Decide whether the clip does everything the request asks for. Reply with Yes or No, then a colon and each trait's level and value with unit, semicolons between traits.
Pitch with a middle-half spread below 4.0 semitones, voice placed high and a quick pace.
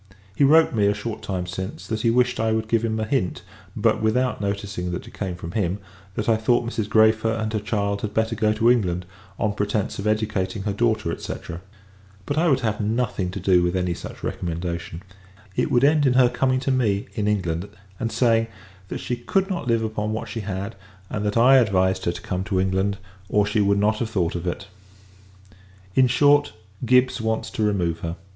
No: average, 3.3 semitones; low, 110 Hz; fast, 210 wpm